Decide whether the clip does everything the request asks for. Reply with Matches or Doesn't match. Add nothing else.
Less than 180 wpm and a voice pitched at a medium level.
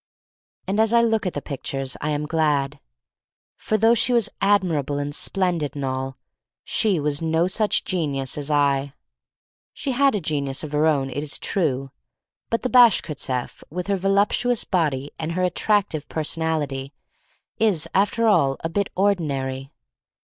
Matches